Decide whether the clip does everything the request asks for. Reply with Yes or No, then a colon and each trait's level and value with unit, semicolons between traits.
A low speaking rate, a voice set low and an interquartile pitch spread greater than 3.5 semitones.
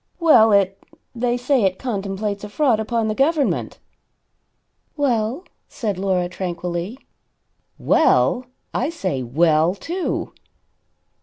No: slow, 105 wpm; high, 215 Hz; average, 5.2 semitones